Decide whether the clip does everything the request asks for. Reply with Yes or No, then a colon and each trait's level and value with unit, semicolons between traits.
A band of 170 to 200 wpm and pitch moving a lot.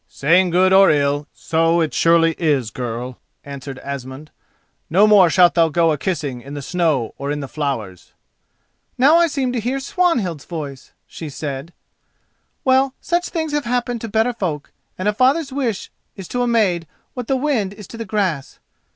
Yes: average, 180 wpm; wide, 8.5 semitones